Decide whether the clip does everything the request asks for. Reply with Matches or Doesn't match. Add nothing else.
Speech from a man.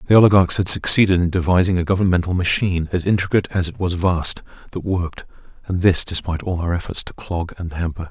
Matches